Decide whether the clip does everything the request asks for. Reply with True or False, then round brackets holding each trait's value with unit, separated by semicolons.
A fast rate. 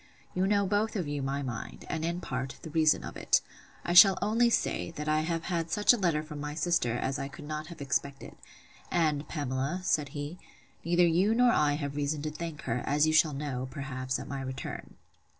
True (215 wpm)